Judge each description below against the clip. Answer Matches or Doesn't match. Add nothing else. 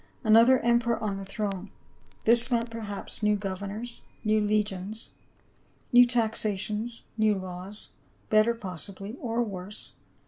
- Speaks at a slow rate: Matches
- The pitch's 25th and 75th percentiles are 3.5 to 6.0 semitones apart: Doesn't match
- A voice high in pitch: Matches